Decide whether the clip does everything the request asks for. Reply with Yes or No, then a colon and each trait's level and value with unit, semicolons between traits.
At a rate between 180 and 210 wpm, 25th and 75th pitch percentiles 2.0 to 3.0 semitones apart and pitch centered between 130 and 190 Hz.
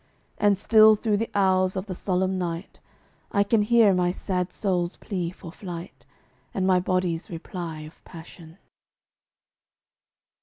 No: average, 140 wpm; narrow, 2.5 semitones; medium, 185 Hz